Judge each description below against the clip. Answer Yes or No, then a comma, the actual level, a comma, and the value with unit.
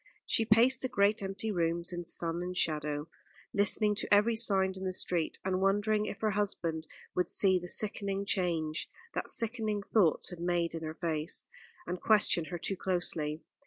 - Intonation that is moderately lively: Yes, average, 3.5 semitones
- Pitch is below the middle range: No, medium, 185 Hz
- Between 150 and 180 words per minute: Yes, average, 175 wpm